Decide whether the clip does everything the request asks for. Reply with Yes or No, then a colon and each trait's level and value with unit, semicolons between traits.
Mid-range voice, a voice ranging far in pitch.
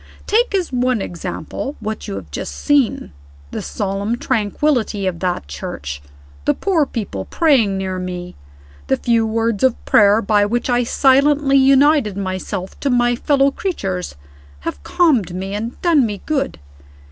No: high, 225 Hz; wide, 6.4 semitones